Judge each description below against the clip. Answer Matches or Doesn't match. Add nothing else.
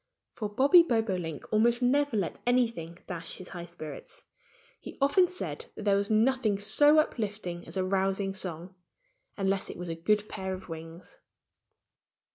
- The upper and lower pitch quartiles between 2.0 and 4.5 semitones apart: Doesn't match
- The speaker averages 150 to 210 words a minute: Matches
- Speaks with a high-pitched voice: Matches